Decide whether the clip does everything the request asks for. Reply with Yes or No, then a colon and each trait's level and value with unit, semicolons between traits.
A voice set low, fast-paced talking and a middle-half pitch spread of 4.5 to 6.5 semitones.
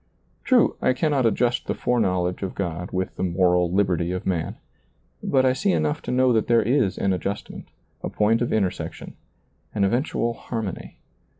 No: low, 105 Hz; average, 170 wpm; average, 5.2 semitones